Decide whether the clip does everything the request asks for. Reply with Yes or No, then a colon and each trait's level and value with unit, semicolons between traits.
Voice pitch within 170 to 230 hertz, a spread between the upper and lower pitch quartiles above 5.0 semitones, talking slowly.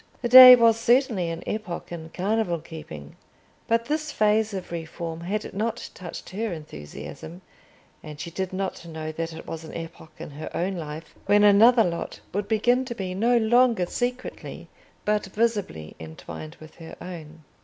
No: medium, 185 Hz; wide, 5.5 semitones; average, 165 wpm